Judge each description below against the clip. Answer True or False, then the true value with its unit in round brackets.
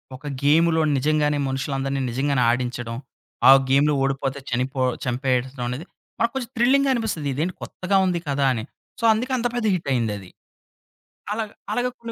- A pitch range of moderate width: False (6.2 semitones)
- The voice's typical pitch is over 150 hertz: False (140 Hz)